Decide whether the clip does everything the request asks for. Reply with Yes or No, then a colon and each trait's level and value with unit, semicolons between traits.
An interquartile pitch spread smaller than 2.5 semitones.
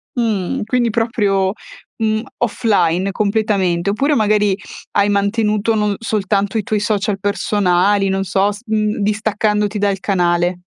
Yes: narrow, 1.9 semitones